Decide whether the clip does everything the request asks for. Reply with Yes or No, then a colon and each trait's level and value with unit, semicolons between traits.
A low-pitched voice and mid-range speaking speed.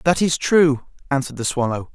No: medium, 145 Hz; average, 185 wpm